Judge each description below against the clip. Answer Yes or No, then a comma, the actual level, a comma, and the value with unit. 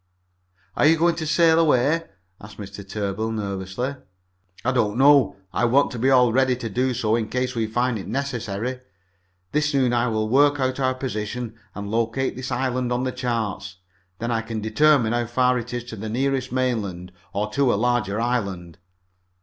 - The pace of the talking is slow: No, average, 185 wpm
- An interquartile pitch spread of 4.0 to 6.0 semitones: No, average, 3.2 semitones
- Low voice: Yes, low, 120 Hz